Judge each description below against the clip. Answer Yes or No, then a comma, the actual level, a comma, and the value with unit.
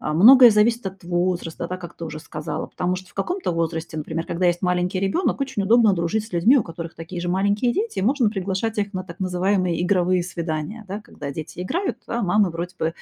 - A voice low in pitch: No, medium, 185 Hz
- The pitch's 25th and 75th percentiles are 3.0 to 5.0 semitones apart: Yes, average, 3.7 semitones